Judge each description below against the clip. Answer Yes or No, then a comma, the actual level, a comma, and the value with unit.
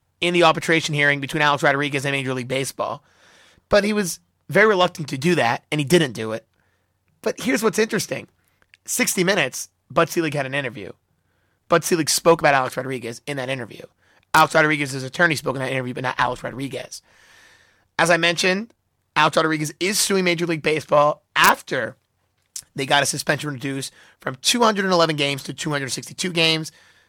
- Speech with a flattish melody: No, average, 4.8 semitones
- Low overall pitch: No, medium, 150 Hz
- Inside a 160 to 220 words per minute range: Yes, average, 170 wpm